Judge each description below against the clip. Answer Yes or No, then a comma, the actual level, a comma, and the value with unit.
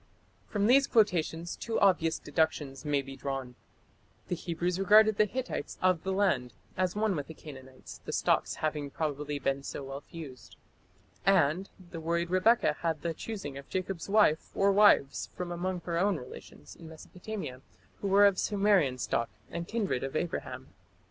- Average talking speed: Yes, average, 170 wpm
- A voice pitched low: No, medium, 170 Hz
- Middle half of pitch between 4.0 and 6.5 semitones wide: Yes, average, 5.3 semitones